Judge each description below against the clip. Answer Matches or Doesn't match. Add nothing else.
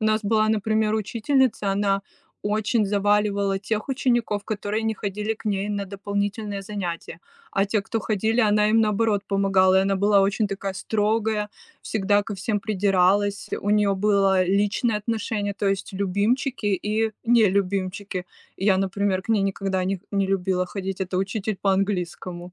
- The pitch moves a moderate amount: Doesn't match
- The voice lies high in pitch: Matches